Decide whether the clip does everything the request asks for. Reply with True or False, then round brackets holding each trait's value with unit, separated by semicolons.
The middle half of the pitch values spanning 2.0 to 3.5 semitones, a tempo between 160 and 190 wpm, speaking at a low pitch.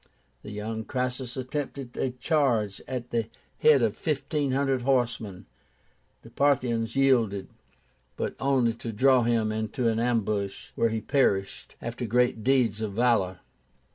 False (3.1 semitones; 140 wpm; 120 Hz)